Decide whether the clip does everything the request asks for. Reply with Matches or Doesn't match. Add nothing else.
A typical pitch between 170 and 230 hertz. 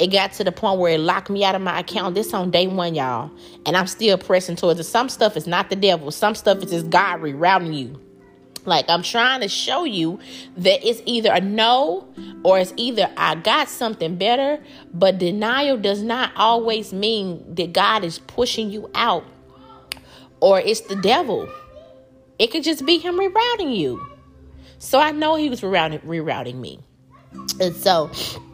Matches